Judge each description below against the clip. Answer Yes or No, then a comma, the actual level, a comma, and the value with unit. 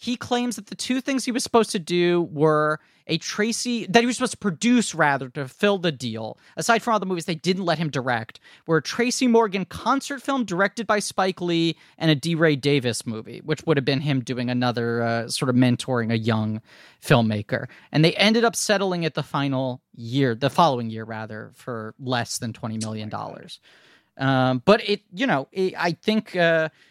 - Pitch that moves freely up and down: Yes, wide, 8.3 semitones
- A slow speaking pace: No, fast, 205 wpm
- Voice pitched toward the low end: No, medium, 160 Hz